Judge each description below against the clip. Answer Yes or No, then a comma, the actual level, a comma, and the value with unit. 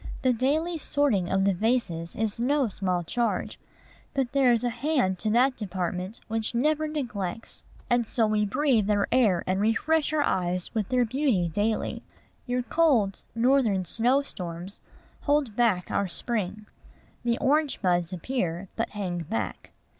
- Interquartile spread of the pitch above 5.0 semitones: Yes, wide, 5.5 semitones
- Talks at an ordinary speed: Yes, average, 155 wpm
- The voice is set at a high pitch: Yes, high, 225 Hz